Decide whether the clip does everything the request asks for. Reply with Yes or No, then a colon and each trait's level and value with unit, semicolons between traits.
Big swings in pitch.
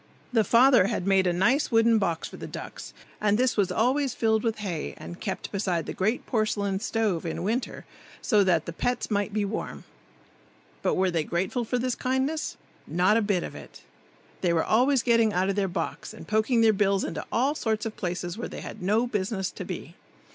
No: average, 3.7 semitones